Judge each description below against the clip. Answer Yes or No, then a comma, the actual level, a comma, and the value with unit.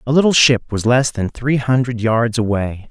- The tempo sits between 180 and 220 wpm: Yes, fast, 205 wpm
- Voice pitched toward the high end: No, low, 120 Hz